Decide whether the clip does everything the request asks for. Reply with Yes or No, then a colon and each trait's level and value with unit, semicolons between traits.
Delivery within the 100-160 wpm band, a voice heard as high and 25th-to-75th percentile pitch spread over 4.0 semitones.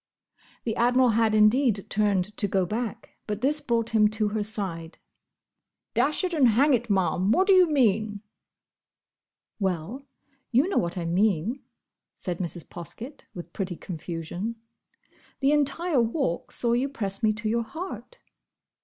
Yes: average, 150 wpm; high, 220 Hz; average, 5.1 semitones